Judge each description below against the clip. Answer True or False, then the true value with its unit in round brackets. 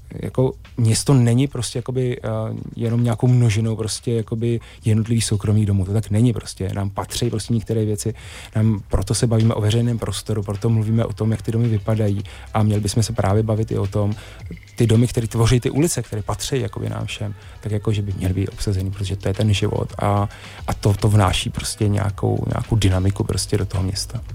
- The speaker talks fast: True (200 wpm)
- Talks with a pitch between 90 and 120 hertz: True (110 Hz)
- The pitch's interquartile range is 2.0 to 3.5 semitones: True (2.4 semitones)